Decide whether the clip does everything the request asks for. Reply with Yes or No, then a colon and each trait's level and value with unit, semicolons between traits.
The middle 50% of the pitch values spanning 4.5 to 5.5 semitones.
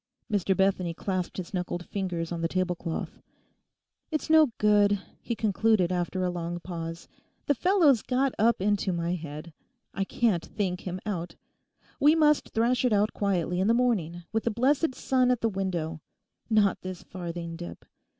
Yes: average, 4.8 semitones